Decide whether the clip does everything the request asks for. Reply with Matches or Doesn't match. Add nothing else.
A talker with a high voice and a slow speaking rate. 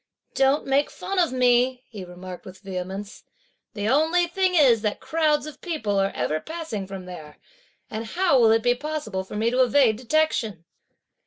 Doesn't match